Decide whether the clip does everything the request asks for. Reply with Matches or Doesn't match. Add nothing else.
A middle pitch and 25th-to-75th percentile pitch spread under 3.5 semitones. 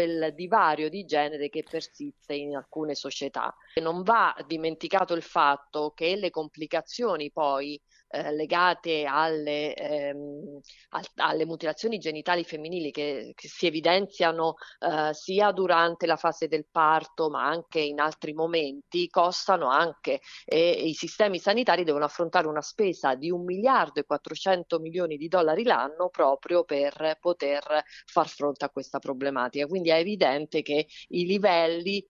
Matches